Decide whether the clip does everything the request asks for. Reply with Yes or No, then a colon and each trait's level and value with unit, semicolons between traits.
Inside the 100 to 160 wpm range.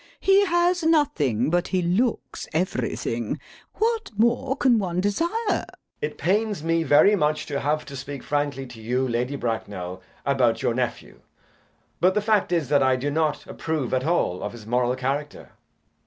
No: average, 170 wpm